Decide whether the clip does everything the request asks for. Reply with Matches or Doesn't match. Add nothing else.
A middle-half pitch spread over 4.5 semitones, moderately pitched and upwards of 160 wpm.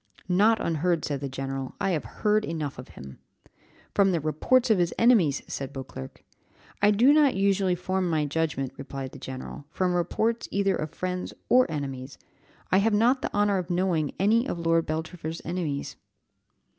Matches